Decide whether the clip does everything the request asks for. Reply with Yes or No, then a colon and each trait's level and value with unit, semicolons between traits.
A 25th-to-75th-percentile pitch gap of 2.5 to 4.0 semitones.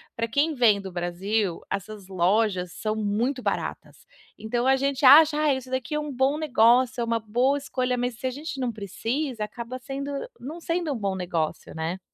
No: average, 4.8 semitones